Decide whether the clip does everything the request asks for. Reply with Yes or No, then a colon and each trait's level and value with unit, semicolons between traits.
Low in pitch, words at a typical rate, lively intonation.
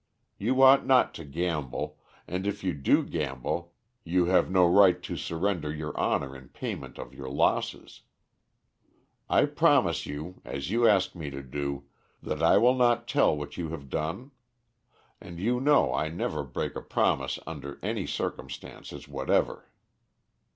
Yes: very low, 85 Hz; average, 155 wpm; wide, 5.7 semitones